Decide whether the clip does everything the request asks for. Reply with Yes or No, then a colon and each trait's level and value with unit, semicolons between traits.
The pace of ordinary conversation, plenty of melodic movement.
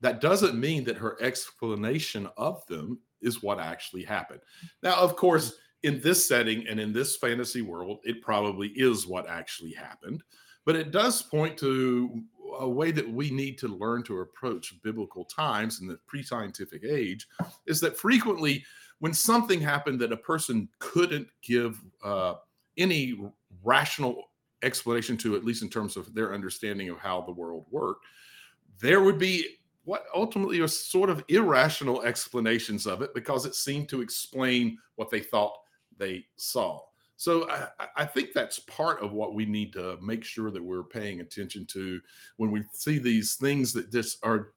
Yes: average, 170 wpm; wide, 5.8 semitones